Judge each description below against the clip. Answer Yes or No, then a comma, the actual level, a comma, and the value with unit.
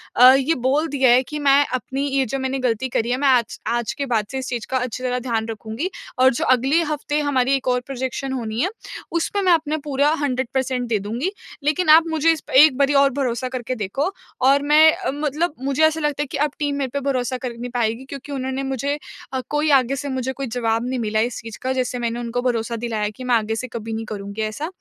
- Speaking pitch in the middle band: No, very high, 260 Hz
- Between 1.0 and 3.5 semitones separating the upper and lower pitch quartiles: Yes, average, 3.1 semitones